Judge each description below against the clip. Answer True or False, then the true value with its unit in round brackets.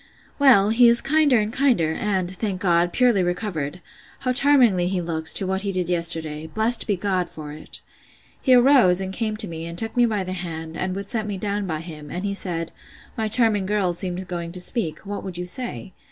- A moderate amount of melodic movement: True (4.1 semitones)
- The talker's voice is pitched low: False (190 Hz)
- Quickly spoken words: True (210 wpm)